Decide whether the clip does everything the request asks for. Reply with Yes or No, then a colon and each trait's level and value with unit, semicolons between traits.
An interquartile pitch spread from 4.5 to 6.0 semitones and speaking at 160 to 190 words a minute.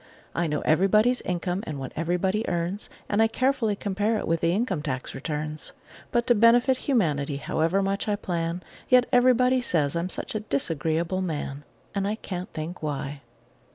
Yes: wide, 5.6 semitones; average, 170 wpm